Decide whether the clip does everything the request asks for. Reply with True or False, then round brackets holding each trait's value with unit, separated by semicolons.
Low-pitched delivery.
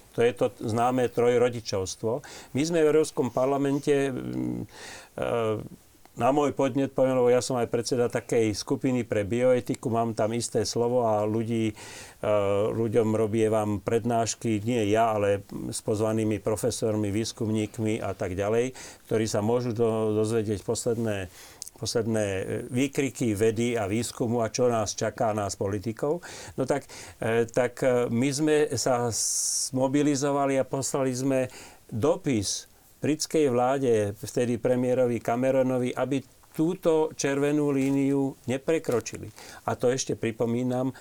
True (120 Hz)